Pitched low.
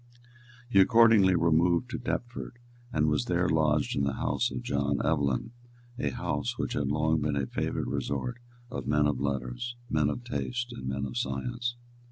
Yes: very low, 75 Hz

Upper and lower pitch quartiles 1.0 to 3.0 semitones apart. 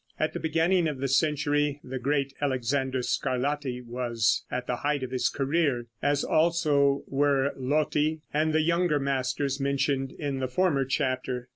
Yes: narrow, 2.5 semitones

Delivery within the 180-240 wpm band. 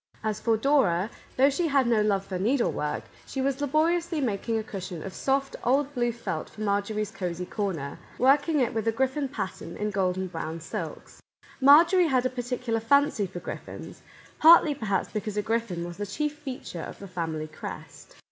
Yes: average, 195 wpm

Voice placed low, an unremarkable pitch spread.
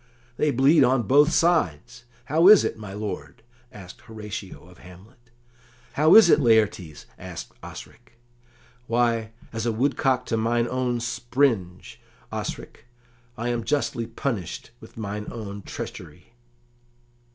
Yes: low, 115 Hz; average, 3.8 semitones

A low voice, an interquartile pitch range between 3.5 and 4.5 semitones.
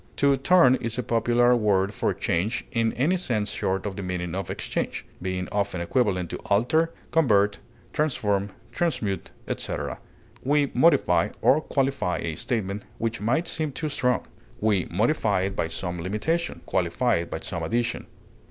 No: low, 110 Hz; wide, 5.6 semitones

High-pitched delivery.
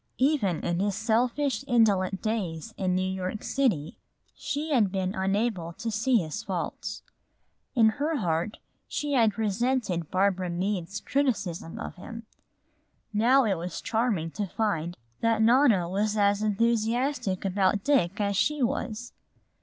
Yes: high, 210 Hz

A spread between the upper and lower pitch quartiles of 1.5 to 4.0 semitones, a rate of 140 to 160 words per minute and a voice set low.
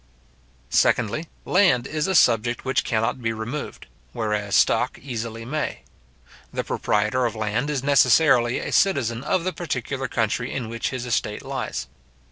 Yes: average, 3.7 semitones; average, 145 wpm; low, 120 Hz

